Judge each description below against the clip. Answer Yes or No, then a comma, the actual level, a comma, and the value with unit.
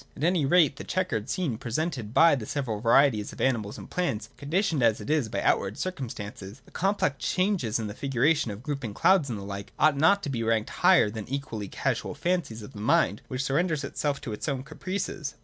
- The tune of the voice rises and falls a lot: Yes, wide, 6.3 semitones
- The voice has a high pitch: No, low, 135 Hz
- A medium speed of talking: No, fast, 220 wpm